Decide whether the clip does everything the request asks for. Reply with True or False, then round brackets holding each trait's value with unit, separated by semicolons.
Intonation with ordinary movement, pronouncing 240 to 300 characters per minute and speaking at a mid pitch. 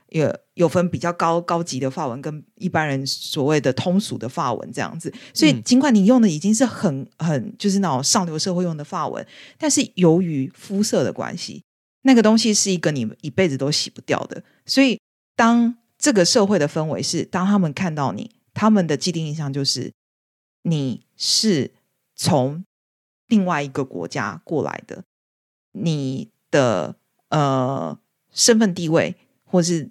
False (6.2 semitones; 245 characters per minute; 170 Hz)